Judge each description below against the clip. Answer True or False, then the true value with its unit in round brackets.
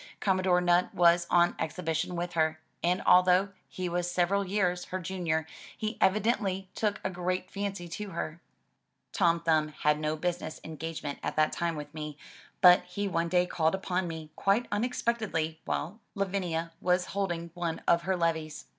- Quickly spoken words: False (165 wpm)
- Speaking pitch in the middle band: True (175 Hz)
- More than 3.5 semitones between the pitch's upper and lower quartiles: False (2.6 semitones)